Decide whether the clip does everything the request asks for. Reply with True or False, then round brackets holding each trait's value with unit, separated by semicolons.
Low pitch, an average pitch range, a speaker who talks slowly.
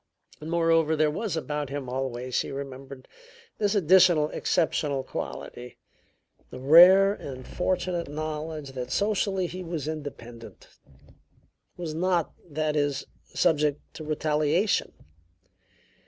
False (155 Hz; 3.6 semitones; 110 wpm)